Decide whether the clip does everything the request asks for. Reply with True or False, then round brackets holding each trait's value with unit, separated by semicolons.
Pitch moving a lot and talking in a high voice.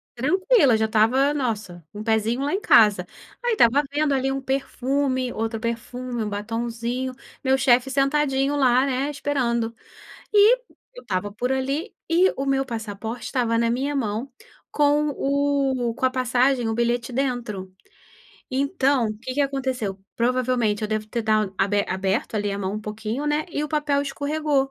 False (3.7 semitones; 255 Hz)